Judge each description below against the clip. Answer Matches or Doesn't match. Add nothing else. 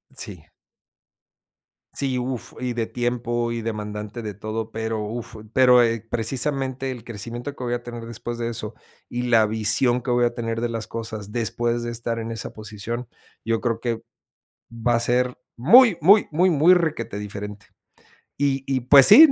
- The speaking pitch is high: Doesn't match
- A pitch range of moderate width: Doesn't match